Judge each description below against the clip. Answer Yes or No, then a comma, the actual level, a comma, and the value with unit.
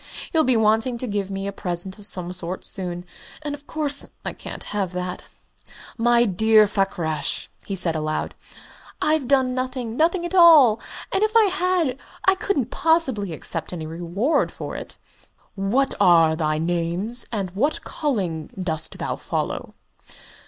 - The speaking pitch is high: Yes, high, 210 Hz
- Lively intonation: Yes, wide, 7.5 semitones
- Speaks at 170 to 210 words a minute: No, average, 160 wpm